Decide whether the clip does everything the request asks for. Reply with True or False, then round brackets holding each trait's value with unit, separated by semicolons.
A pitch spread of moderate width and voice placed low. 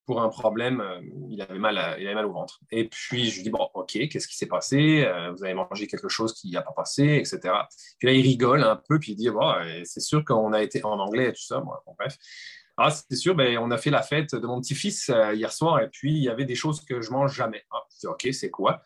True (4.8 semitones; 130 Hz)